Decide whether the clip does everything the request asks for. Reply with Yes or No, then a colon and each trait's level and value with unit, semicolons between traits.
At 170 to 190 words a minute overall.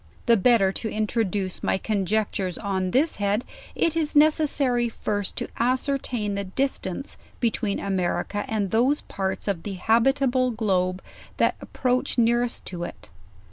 No: average, 140 wpm